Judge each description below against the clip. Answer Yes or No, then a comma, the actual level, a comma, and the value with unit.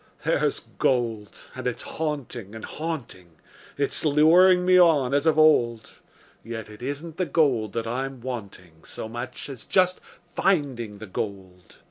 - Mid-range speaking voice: No, low, 130 Hz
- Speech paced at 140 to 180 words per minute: Yes, average, 145 wpm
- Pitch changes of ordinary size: No, wide, 6.0 semitones